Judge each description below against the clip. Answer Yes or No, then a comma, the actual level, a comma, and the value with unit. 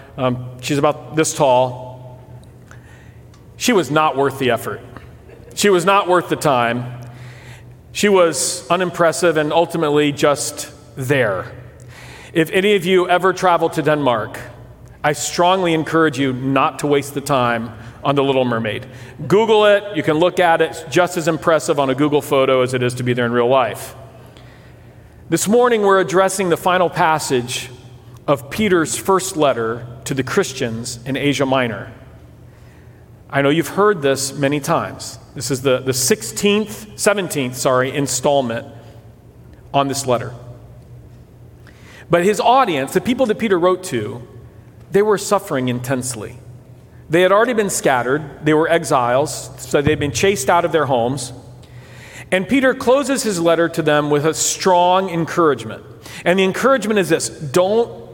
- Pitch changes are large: Yes, wide, 5.9 semitones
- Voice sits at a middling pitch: Yes, medium, 145 Hz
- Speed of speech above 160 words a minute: No, average, 155 wpm